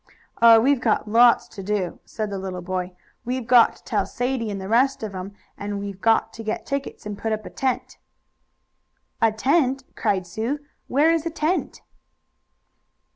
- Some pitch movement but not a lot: Yes, average, 4.4 semitones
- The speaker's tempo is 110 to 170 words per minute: No, average, 180 wpm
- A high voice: Yes, high, 225 Hz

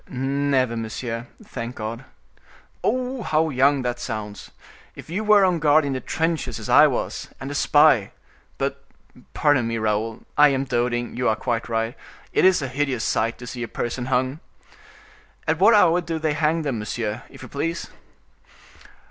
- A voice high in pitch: No, low, 135 Hz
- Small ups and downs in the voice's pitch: No, average, 4.9 semitones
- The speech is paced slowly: No, average, 165 wpm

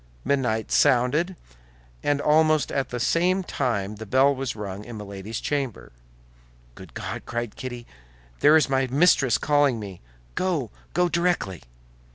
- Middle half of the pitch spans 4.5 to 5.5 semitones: Yes, average, 5.2 semitones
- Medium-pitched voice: No, low, 130 Hz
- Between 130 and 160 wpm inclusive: Yes, average, 140 wpm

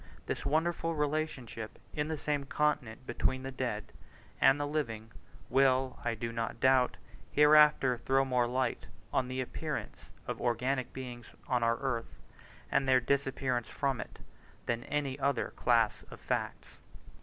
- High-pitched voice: No, low, 130 Hz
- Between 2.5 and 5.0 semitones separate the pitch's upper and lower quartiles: Yes, average, 2.8 semitones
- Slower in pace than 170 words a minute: Yes, average, 145 wpm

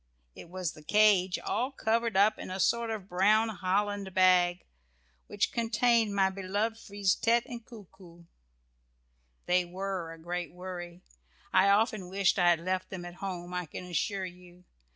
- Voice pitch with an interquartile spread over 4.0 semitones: No, average, 2.9 semitones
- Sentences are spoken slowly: No, average, 165 wpm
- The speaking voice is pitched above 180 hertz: Yes, high, 190 Hz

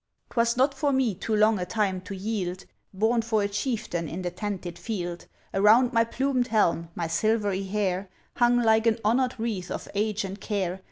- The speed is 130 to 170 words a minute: No, average, 185 wpm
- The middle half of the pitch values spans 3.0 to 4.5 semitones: Yes, average, 3.6 semitones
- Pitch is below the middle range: No, high, 210 Hz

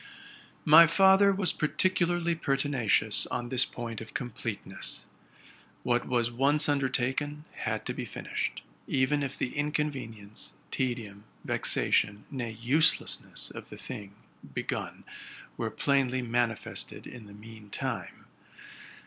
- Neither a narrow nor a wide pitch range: Yes, average, 4.6 semitones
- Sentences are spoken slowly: Yes, slow, 115 wpm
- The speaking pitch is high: No, low, 130 Hz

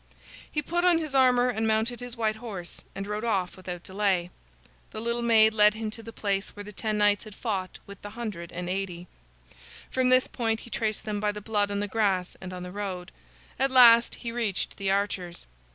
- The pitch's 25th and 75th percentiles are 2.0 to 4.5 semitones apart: Yes, average, 3.1 semitones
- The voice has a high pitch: Yes, high, 210 Hz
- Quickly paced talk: Yes, fast, 215 wpm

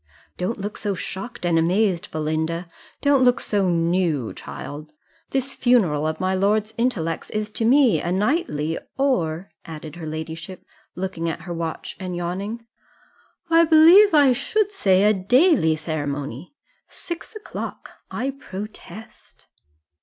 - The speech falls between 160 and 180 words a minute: No, slow, 135 wpm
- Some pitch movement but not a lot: No, wide, 7.0 semitones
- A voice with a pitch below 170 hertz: No, high, 190 Hz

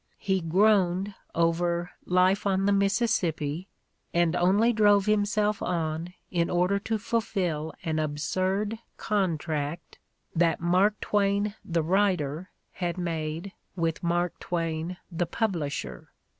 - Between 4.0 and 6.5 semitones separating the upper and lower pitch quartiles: No, average, 3.3 semitones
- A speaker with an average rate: No, slow, 115 wpm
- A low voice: No, medium, 180 Hz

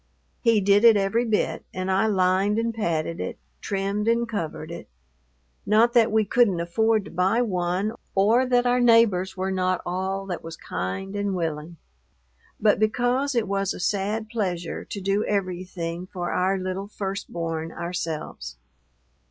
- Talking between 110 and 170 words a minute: Yes, average, 160 wpm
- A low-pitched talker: No, high, 195 Hz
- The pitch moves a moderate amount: Yes, average, 3.5 semitones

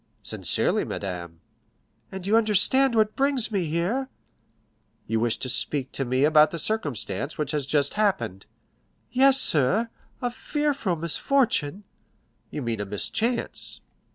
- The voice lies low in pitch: No, medium, 170 Hz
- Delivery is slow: Yes, slow, 125 wpm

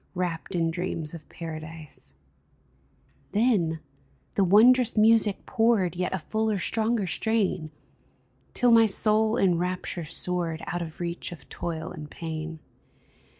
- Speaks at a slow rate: Yes, slow, 125 wpm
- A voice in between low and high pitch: Yes, medium, 180 Hz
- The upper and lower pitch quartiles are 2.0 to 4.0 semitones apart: No, average, 4.9 semitones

